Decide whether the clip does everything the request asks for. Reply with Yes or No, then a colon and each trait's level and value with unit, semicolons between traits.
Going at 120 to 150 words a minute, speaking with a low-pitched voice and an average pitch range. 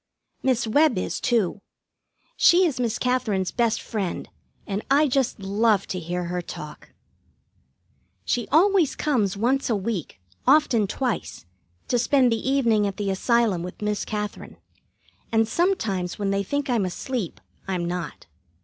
No: average, 145 wpm; high, 225 Hz; average, 4.8 semitones